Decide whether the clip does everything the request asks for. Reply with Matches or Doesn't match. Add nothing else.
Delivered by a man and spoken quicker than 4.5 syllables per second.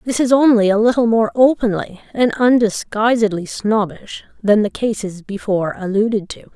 Doesn't match